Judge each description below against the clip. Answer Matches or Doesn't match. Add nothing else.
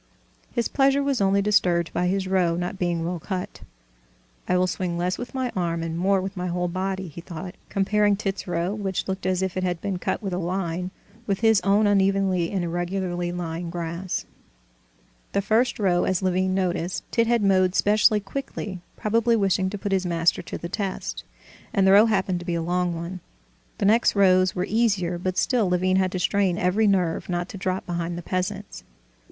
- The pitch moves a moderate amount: Doesn't match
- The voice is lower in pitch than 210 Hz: Matches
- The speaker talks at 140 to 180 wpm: Doesn't match